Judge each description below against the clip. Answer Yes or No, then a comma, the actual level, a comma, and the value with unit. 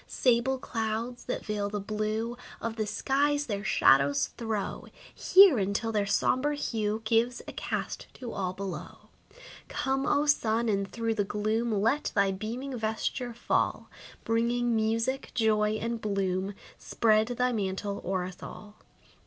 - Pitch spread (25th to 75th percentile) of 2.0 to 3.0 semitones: Yes, average, 2.7 semitones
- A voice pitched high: Yes, high, 220 Hz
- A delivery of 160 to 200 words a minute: No, average, 145 wpm